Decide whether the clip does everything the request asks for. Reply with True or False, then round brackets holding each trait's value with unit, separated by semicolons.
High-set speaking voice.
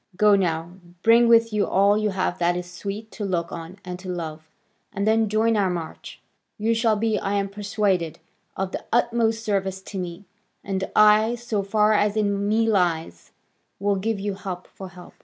True (200 Hz)